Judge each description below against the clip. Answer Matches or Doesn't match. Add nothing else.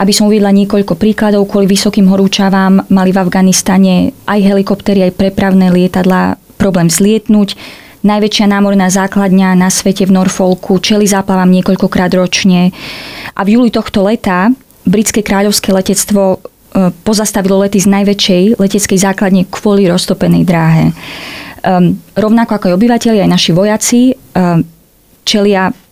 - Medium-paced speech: Matches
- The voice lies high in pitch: Matches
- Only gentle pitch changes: Matches